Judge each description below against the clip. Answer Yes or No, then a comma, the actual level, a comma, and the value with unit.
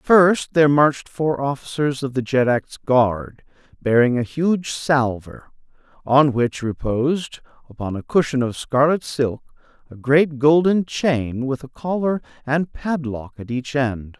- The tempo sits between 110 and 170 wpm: Yes, average, 145 wpm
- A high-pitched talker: No, low, 135 Hz